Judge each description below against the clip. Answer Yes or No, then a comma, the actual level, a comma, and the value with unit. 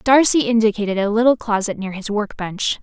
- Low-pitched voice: No, high, 215 Hz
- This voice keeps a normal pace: Yes, average, 190 wpm